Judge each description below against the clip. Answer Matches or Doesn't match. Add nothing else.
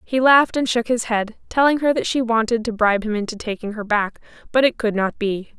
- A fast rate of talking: Matches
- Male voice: Doesn't match